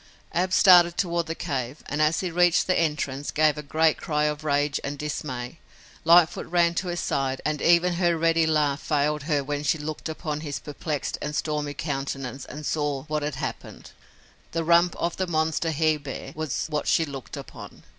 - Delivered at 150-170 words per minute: No, average, 190 wpm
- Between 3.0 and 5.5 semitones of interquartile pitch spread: No, narrow, 2.5 semitones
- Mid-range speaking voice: Yes, medium, 155 Hz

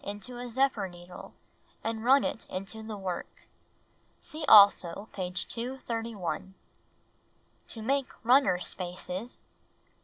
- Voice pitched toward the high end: Yes, high, 220 Hz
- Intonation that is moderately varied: Yes, average, 4.8 semitones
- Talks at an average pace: No, slow, 125 wpm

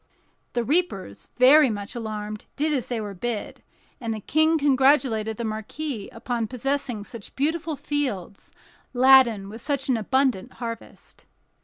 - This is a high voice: Yes, high, 245 Hz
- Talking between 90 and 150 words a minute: Yes, average, 140 wpm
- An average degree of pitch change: Yes, average, 4.5 semitones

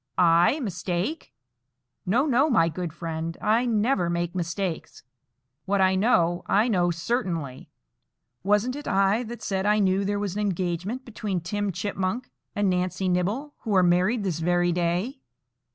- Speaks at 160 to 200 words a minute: No, average, 150 wpm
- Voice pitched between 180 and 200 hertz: Yes, high, 190 Hz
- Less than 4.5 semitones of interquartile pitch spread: Yes, average, 3.5 semitones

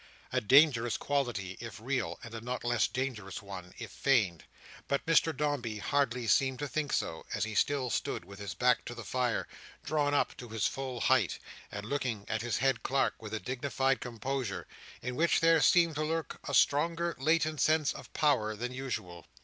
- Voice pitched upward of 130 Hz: No, low, 125 Hz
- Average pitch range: Yes, average, 4.6 semitones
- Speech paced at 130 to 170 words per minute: No, average, 190 wpm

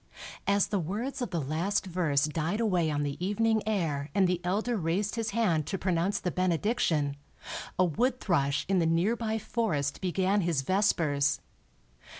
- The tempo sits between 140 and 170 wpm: Yes, average, 160 wpm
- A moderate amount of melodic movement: Yes, average, 4.7 semitones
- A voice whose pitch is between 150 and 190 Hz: Yes, medium, 185 Hz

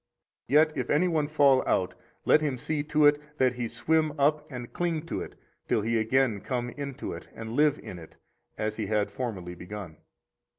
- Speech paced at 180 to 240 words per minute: Yes, average, 195 wpm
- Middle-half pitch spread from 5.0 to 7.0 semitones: Yes, wide, 5.4 semitones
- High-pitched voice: No, low, 130 Hz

